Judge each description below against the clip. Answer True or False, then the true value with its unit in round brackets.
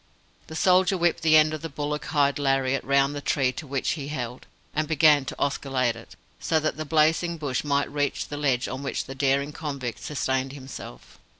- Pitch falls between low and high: True (145 Hz)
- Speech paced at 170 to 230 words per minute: True (200 wpm)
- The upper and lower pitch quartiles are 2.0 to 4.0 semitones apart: True (2.4 semitones)